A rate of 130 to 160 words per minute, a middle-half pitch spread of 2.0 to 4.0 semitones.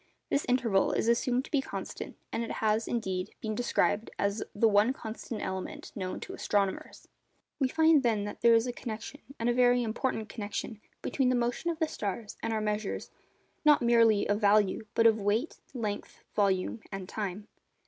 No: average, 180 wpm; average, 3.0 semitones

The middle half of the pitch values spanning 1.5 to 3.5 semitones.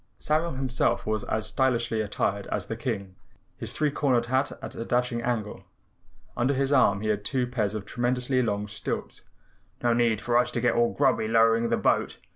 Yes: average, 2.7 semitones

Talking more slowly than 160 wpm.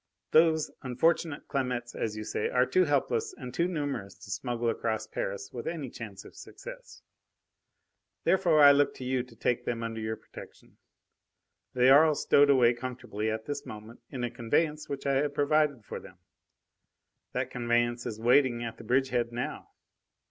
No: average, 170 wpm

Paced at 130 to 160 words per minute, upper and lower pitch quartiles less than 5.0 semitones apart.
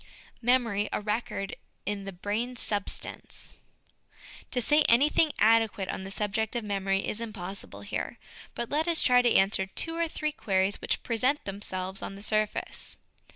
Yes: average, 155 wpm; average, 4.0 semitones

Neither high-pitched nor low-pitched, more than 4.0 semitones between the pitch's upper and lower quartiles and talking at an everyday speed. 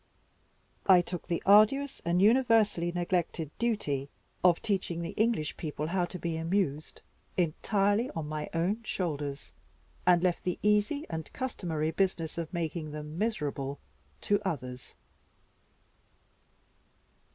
No: medium, 175 Hz; average, 4.6 semitones; slow, 120 wpm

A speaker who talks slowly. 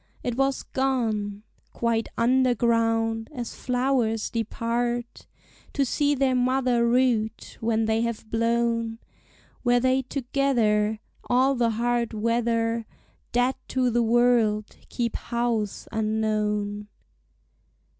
Yes: slow, 105 wpm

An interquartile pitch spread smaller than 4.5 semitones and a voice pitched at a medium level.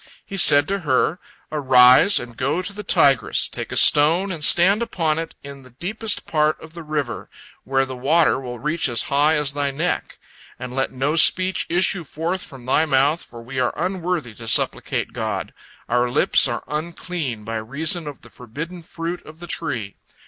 No: average, 4.8 semitones; medium, 150 Hz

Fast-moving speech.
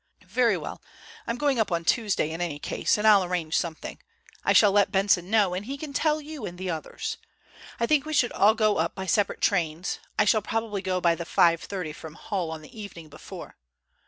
Yes: fast, 215 wpm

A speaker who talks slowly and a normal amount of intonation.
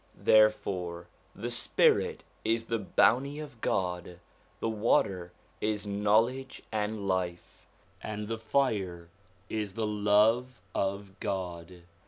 Yes: slow, 110 wpm; average, 3.3 semitones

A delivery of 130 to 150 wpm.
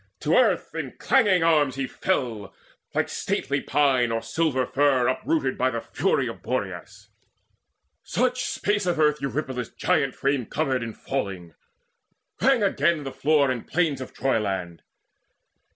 Yes: average, 140 wpm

